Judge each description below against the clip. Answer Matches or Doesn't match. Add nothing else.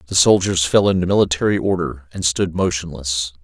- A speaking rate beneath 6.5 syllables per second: Matches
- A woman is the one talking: Doesn't match